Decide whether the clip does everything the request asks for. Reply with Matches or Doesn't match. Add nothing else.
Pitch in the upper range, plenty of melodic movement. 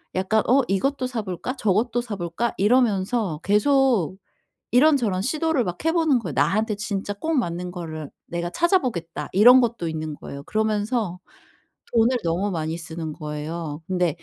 Matches